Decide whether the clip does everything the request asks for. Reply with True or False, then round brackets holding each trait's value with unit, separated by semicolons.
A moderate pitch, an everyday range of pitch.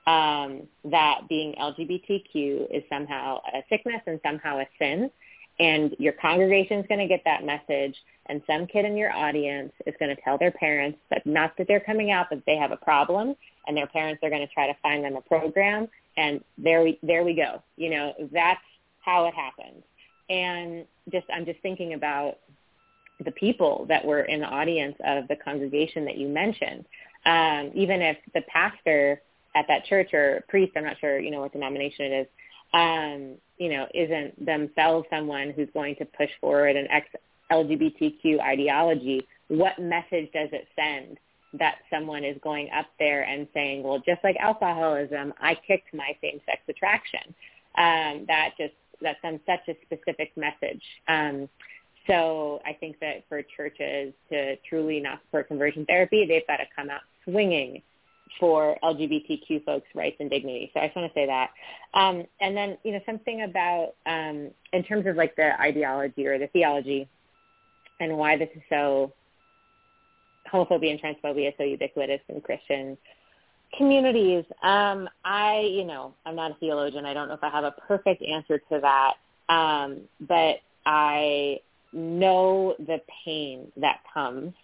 True (155 Hz; 3.6 semitones)